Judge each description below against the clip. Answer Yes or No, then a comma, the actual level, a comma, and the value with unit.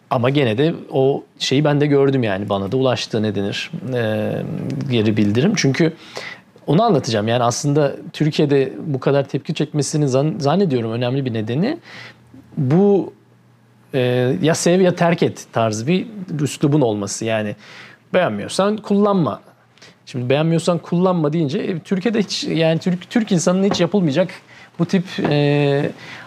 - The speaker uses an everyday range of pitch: No, wide, 5.9 semitones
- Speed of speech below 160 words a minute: Yes, fast, 140 wpm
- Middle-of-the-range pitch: Yes, medium, 145 Hz